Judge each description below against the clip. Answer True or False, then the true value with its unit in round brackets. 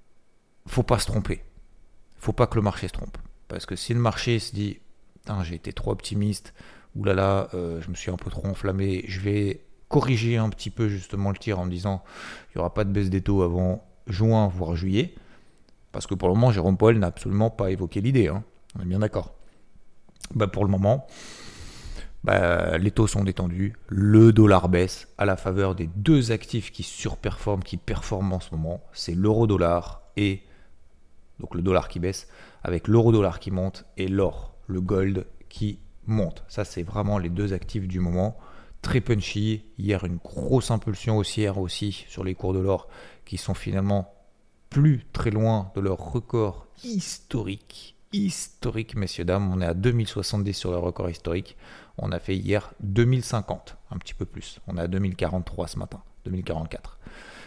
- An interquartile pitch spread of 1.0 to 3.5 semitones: True (3.0 semitones)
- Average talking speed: True (185 wpm)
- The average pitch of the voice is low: True (100 Hz)